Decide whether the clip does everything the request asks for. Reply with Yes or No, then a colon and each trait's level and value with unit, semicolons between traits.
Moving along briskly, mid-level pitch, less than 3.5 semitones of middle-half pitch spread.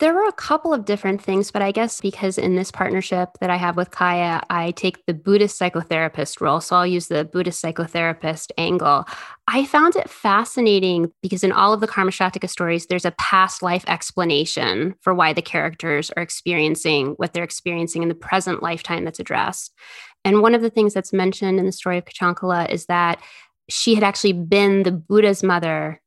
No: average, 195 wpm; medium, 180 Hz; narrow, 2.6 semitones